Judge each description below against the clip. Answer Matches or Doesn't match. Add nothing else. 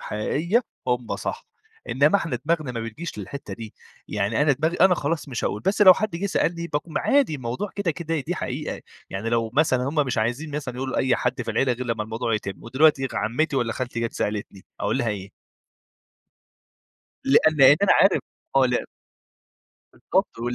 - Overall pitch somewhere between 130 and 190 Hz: Matches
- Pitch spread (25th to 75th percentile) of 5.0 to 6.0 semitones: Matches